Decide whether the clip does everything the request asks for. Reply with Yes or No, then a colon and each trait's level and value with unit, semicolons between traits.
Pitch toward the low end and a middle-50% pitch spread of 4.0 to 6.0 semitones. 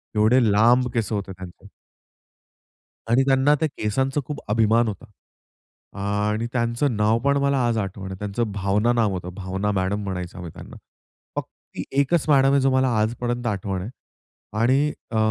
Yes: low, 110 Hz; average, 4.7 semitones